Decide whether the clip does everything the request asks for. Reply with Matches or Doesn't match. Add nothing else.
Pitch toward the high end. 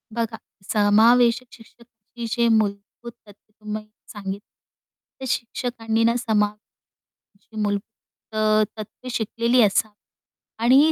Matches